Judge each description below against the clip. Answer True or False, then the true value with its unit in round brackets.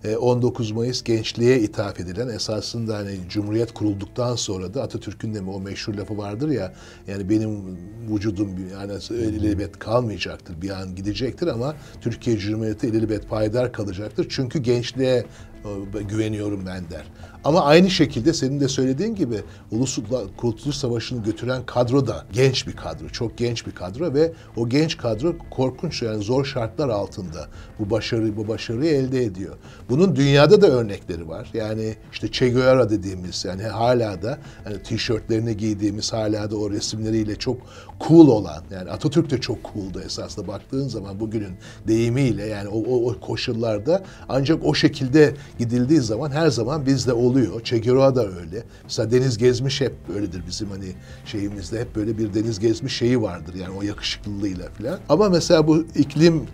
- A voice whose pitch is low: True (110 Hz)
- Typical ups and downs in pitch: True (3.7 semitones)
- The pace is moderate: False (160 wpm)